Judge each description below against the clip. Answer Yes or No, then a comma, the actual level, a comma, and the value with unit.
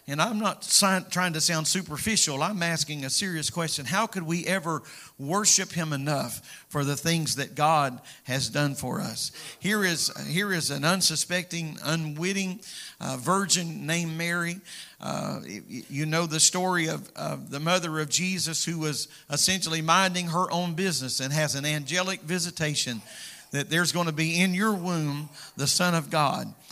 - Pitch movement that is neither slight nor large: Yes, average, 3.4 semitones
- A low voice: No, medium, 165 Hz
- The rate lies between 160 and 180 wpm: Yes, average, 165 wpm